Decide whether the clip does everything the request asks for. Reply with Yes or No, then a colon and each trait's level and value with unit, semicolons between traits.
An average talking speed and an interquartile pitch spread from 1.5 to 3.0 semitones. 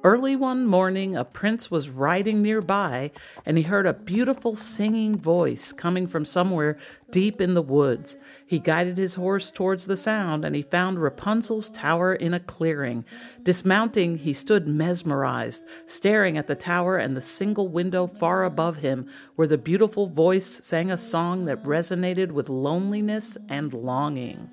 No: average, 160 wpm; average, 4.2 semitones